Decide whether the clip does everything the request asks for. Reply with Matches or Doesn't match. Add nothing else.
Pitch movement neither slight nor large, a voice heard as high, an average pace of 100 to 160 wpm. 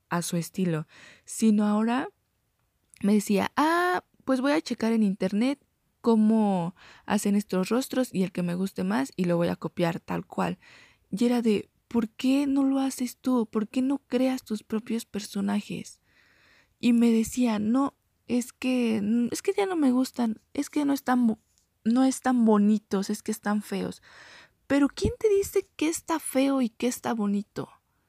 Doesn't match